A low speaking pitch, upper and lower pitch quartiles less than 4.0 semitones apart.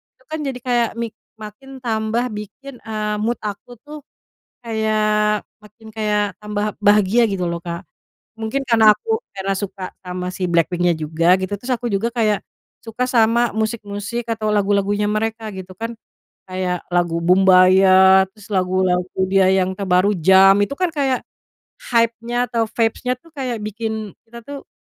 No: high, 210 Hz; average, 3.5 semitones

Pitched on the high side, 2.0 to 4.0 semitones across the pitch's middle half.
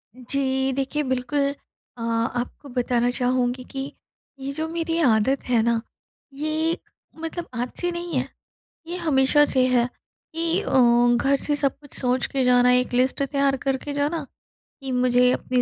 Yes: very high, 265 Hz; average, 2.8 semitones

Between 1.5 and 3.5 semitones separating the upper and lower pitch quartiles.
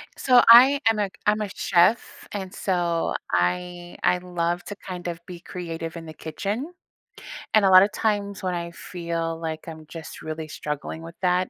Yes: average, 3.2 semitones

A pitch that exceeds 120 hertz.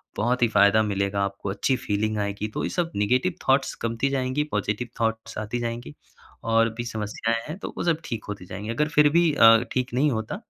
No: low, 115 Hz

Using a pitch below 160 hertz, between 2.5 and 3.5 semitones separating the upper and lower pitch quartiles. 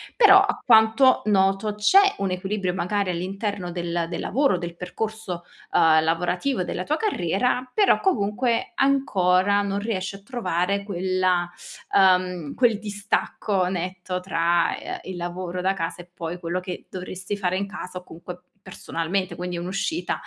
No: medium, 185 Hz; average, 2.8 semitones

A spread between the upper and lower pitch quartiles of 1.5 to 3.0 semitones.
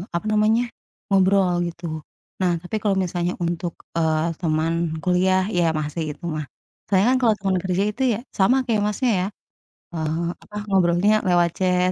Yes: narrow, 2.5 semitones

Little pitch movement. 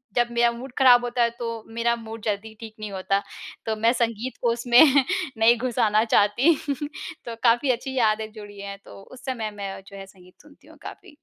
Yes: narrow, 2.3 semitones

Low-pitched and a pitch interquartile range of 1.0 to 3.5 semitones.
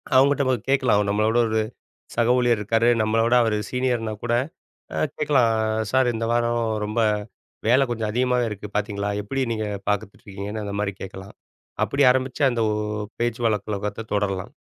Yes: low, 115 Hz; average, 2.9 semitones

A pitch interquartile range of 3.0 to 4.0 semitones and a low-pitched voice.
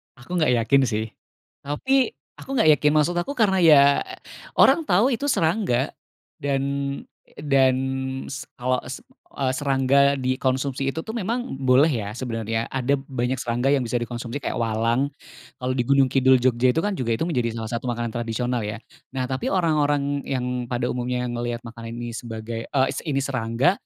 Yes: average, 3.3 semitones; low, 130 Hz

